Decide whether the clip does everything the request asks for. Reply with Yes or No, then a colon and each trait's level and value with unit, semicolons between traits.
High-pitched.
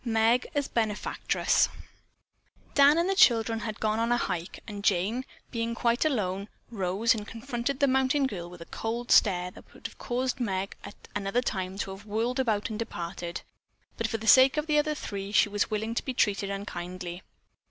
Yes: high, 225 Hz